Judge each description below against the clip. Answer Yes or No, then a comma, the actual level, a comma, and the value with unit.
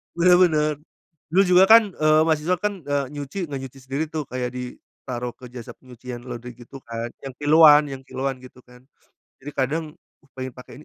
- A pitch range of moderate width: Yes, average, 3.7 semitones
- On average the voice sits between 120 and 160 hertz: Yes, low, 135 Hz